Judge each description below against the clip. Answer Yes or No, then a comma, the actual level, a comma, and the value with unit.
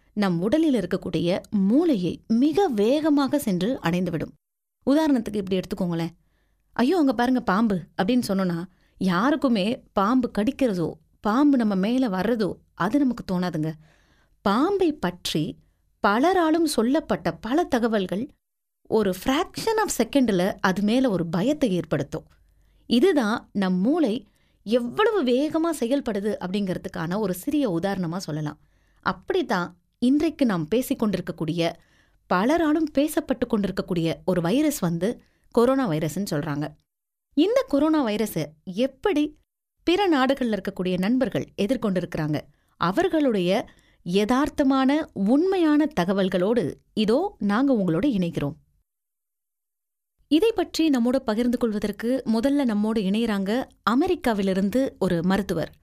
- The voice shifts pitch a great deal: Yes, wide, 6.9 semitones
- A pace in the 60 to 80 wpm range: No, average, 100 wpm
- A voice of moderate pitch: No, high, 225 Hz